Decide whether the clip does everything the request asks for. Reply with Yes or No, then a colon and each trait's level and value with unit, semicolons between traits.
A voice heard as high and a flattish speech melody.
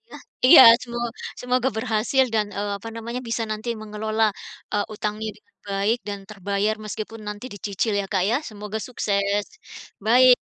Yes: high, 215 Hz; narrow, 2.0 semitones